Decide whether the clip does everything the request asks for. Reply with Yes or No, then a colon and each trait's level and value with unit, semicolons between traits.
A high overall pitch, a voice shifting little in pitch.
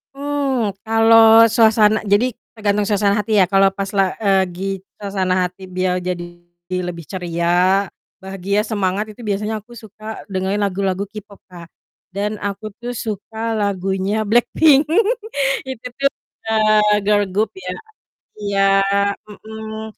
Yes: high, 205 Hz; narrow, 2.3 semitones